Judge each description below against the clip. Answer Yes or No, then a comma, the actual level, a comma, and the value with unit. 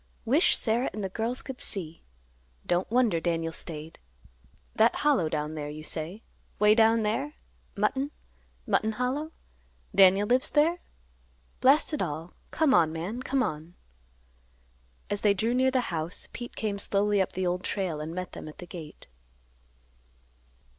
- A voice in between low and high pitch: No, high, 205 Hz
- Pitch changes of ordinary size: No, wide, 6.8 semitones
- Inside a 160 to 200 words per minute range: No, average, 150 wpm